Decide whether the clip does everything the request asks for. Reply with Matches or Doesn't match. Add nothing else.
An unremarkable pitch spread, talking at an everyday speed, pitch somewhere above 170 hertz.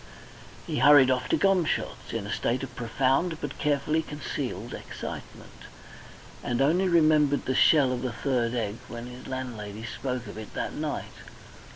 Doesn't match